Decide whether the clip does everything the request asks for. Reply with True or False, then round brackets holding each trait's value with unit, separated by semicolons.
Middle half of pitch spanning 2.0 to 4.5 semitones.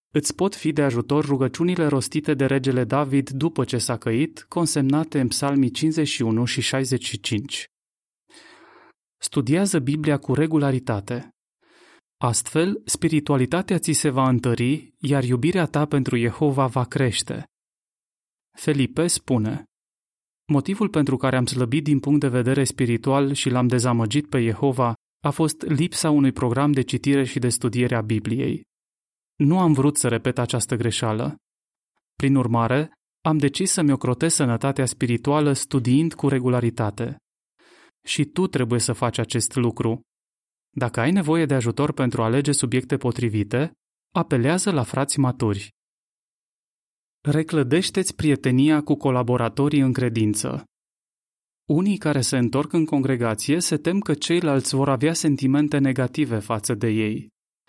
True (3.4 semitones)